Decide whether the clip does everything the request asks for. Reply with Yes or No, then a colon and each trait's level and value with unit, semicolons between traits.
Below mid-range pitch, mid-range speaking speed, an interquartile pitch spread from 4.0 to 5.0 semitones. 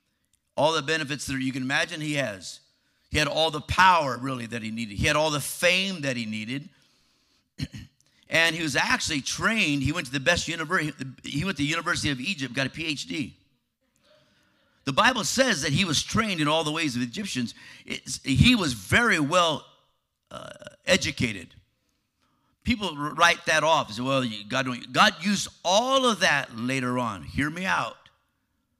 No: medium, 150 Hz; average, 180 wpm; average, 4.6 semitones